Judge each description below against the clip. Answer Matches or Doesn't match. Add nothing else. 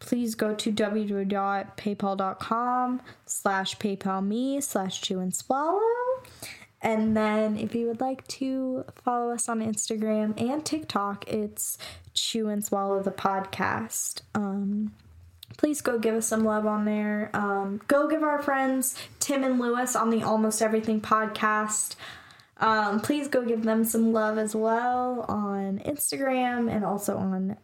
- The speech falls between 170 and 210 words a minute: Doesn't match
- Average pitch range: Matches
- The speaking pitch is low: Doesn't match